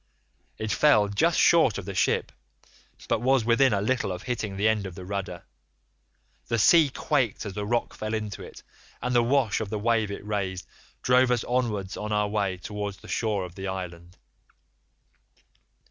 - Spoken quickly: No, average, 180 wpm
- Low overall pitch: Yes, low, 105 Hz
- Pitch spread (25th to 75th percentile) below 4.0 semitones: Yes, average, 3.4 semitones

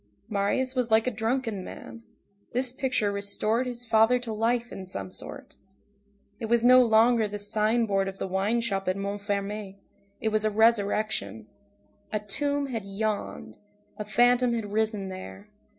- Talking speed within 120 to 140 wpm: No, average, 155 wpm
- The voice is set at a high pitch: Yes, high, 220 Hz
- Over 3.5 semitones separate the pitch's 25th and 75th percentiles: No, average, 2.8 semitones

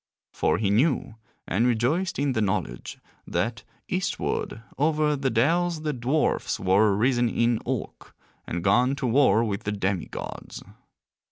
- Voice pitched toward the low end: Yes, low, 120 Hz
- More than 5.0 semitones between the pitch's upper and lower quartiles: Yes, wide, 5.4 semitones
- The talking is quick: No, average, 145 wpm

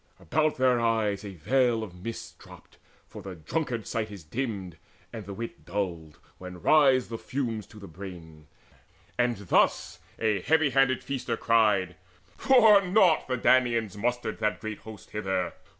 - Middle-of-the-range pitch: No, low, 110 Hz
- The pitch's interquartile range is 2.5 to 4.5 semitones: No, average, 4.9 semitones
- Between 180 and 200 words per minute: No, average, 155 wpm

